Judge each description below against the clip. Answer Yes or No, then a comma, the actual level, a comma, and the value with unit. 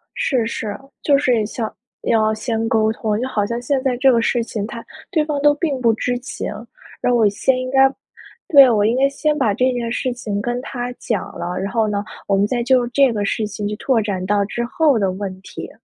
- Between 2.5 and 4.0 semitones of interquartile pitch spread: Yes, average, 3.4 semitones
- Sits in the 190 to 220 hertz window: No, high, 235 Hz